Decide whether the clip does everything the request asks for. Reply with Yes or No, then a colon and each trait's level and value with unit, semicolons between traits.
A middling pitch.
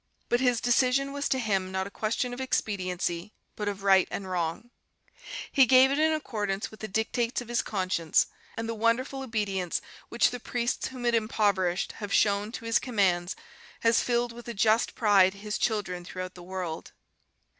No: high, 215 Hz